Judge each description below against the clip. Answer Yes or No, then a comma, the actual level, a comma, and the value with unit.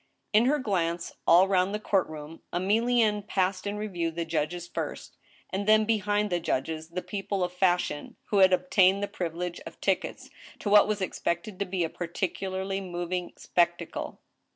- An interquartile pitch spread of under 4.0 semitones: Yes, average, 2.8 semitones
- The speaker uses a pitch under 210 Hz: Yes, medium, 185 Hz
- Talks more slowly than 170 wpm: No, average, 175 wpm